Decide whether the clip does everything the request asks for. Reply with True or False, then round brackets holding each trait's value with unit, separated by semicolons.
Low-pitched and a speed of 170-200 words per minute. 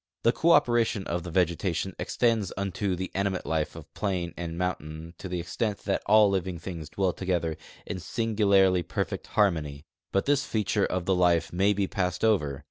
True (95 Hz; 185 wpm)